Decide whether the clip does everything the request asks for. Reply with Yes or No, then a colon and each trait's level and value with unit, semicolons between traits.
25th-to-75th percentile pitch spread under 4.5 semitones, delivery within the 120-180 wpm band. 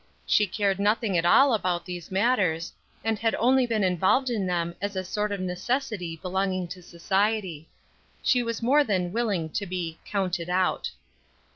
Yes: average, 3.8 semitones; average, 165 wpm